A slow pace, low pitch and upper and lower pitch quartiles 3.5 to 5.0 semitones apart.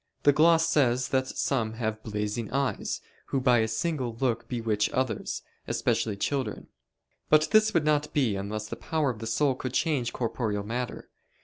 No: average, 170 wpm; low, 125 Hz; average, 4.5 semitones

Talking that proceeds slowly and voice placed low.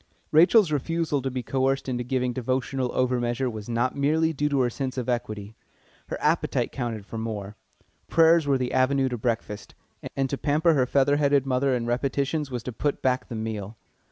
No: average, 185 wpm; low, 130 Hz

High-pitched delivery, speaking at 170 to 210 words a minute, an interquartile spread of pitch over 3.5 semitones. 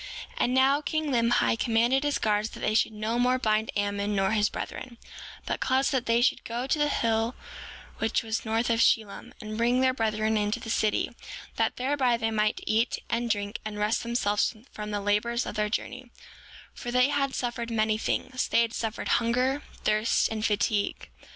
No: high, 230 Hz; average, 190 wpm; average, 2.7 semitones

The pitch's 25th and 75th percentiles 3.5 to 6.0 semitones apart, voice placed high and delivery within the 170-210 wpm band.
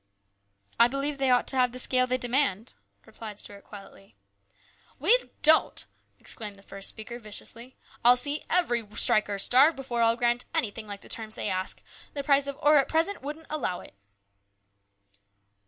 Yes: average, 4.7 semitones; high, 245 Hz; average, 180 wpm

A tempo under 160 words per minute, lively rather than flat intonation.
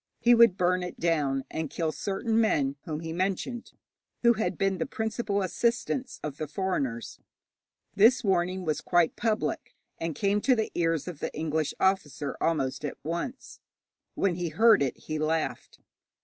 No: average, 165 wpm; wide, 5.7 semitones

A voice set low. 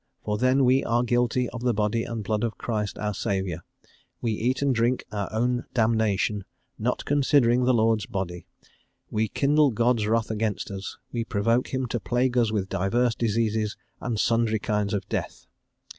Yes: low, 115 Hz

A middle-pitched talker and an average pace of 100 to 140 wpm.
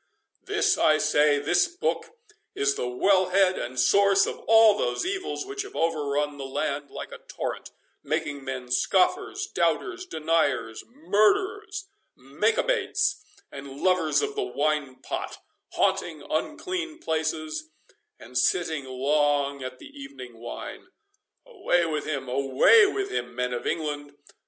Yes: medium, 155 Hz; slow, 135 wpm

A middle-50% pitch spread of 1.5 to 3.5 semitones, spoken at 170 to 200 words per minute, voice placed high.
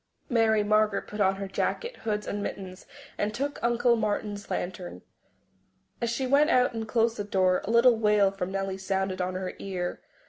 Yes: average, 3.2 semitones; average, 180 wpm; high, 210 Hz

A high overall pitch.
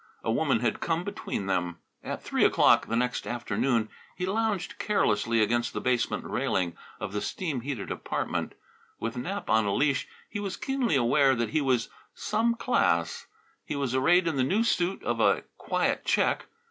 No: low, 130 Hz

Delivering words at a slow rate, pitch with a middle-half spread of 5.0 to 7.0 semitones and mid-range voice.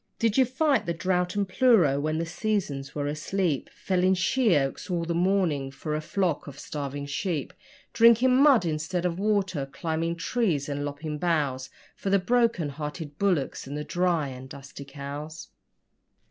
No: average, 160 wpm; average, 5.3 semitones; medium, 165 Hz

